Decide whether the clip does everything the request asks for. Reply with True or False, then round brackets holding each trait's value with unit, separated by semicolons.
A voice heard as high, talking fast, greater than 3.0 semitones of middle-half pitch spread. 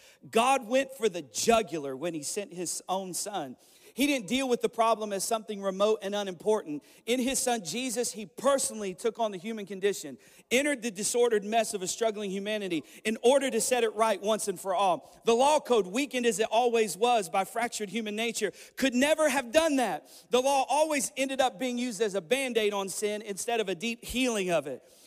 True (225 Hz; 210 wpm; 3.7 semitones)